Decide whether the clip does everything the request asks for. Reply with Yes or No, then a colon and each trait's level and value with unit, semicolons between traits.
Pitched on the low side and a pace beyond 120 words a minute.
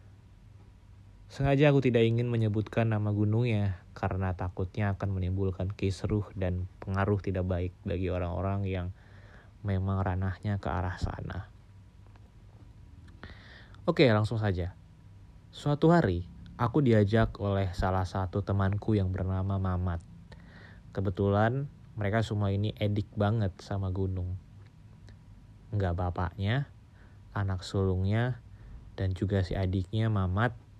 No: low, 100 Hz; average, 105 wpm